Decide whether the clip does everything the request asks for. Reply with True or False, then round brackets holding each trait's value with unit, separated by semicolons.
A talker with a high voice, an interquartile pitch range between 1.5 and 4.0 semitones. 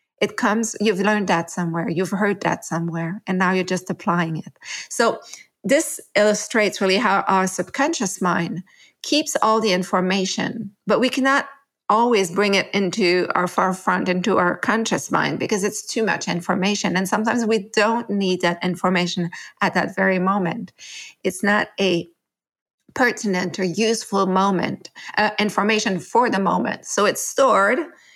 True (195 Hz; 2.7 semitones)